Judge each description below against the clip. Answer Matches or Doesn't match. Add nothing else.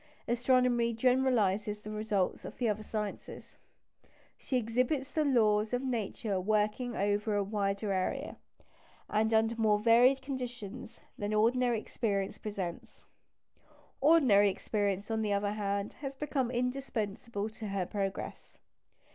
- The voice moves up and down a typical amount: Matches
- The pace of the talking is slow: Matches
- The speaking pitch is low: Doesn't match